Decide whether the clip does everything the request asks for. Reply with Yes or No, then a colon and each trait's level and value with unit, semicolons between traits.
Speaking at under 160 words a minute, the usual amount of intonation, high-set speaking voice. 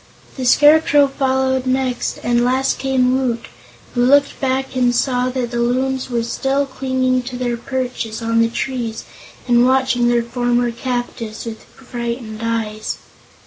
No: average, 145 wpm; narrow, 1.8 semitones; very high, 250 Hz